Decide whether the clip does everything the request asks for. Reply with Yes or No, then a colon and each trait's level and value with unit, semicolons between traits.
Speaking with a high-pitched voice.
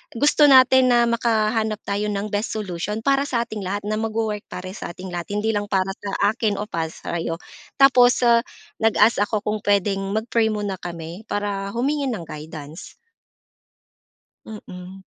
Yes: high, 210 Hz